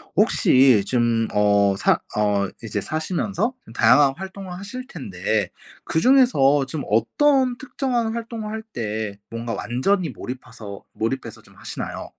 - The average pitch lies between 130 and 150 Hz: Yes, low, 135 Hz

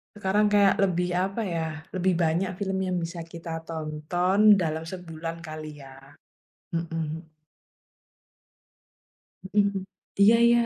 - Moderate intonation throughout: Yes, average, 3.1 semitones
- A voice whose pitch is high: No, medium, 175 Hz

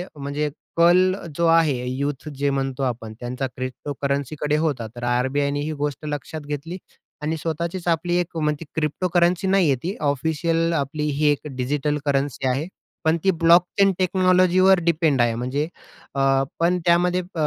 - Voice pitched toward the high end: No, medium, 150 Hz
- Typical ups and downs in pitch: Yes, average, 3.6 semitones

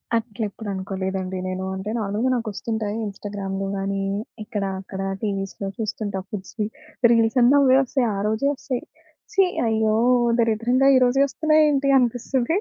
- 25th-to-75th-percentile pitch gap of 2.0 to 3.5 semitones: No, average, 3.9 semitones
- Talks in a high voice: Yes, high, 220 Hz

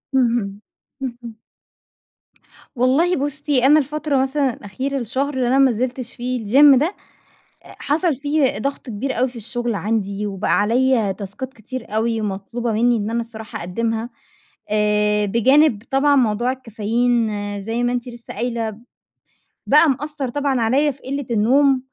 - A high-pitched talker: Yes, high, 245 Hz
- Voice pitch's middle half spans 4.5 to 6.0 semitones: No, average, 3.5 semitones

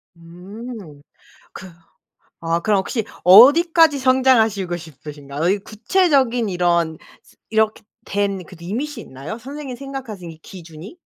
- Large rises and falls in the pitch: Yes, wide, 7.1 semitones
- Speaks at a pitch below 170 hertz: No, high, 205 Hz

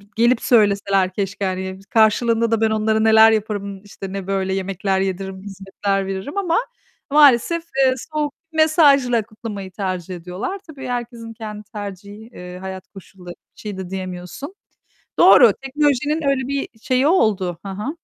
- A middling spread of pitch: Yes, average, 4.6 semitones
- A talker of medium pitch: No, high, 210 Hz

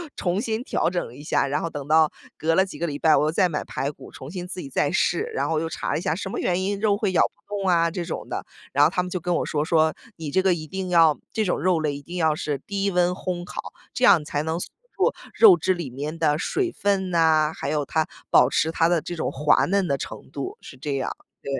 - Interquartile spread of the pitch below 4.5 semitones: Yes, average, 3.5 semitones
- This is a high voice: No, medium, 165 Hz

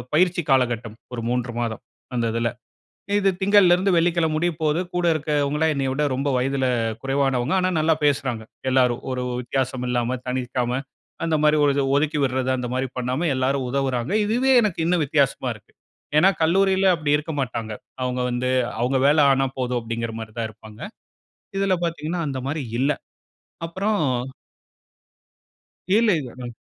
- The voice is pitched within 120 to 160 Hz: Yes, low, 135 Hz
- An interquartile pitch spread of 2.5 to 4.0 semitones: No, average, 4.4 semitones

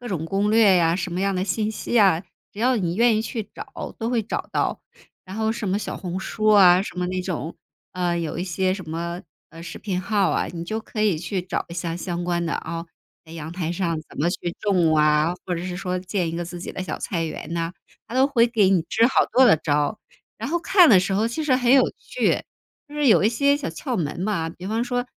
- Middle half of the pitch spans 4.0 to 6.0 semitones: Yes, average, 4.4 semitones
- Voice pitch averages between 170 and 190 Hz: Yes, medium, 185 Hz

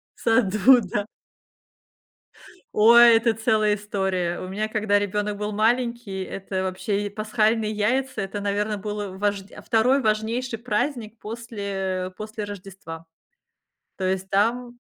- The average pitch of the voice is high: Yes, high, 210 Hz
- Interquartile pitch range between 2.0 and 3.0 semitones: Yes, narrow, 2.4 semitones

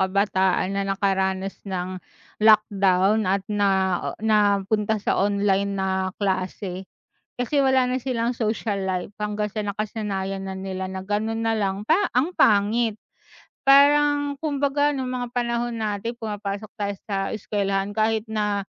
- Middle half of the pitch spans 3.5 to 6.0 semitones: No, average, 2.9 semitones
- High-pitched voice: Yes, high, 205 Hz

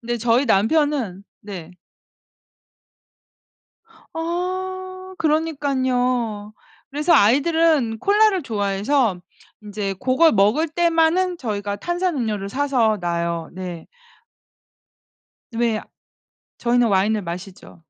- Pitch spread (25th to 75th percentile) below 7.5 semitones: No, wide, 8.0 semitones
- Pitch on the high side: Yes, high, 240 Hz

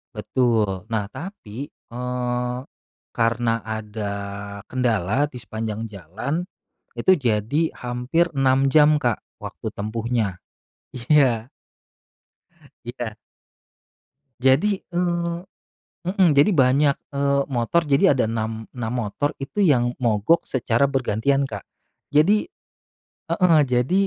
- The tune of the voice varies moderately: Yes, average, 4.3 semitones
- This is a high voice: No, low, 125 Hz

